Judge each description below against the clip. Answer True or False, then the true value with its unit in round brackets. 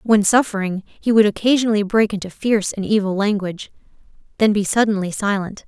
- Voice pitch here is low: False (205 Hz)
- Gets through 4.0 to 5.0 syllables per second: False (6.0 syllables/s)